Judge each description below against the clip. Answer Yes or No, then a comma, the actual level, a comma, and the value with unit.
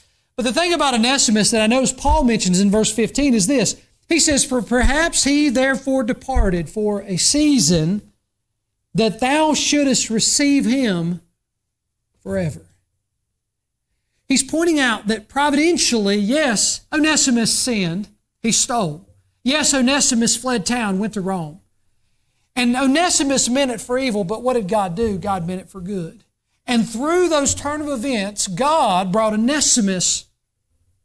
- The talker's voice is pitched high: Yes, high, 230 Hz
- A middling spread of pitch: No, wide, 6.3 semitones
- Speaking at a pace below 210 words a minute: Yes, average, 140 wpm